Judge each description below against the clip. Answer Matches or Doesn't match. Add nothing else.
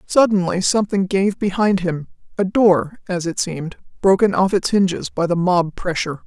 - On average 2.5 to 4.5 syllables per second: Doesn't match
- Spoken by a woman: Matches